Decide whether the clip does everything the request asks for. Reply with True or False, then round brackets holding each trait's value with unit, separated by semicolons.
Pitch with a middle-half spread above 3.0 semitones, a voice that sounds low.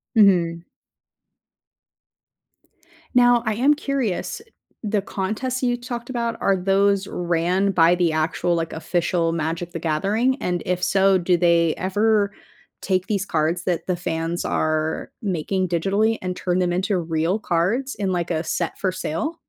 False (3.7 semitones; 185 Hz)